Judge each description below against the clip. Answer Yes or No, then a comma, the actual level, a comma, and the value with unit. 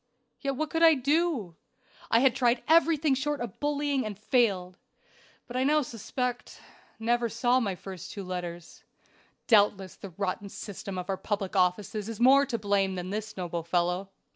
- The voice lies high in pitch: Yes, high, 220 Hz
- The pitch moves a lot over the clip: Yes, wide, 5.8 semitones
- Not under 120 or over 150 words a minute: No, average, 165 wpm